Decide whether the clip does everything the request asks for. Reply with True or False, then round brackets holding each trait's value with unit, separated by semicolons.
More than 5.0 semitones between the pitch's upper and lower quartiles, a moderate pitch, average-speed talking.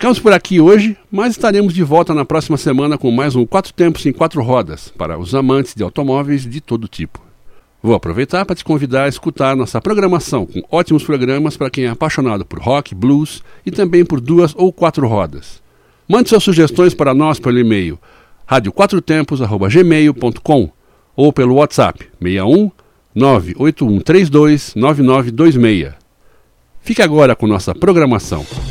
True (5.6 semitones; 145 Hz; 145 wpm)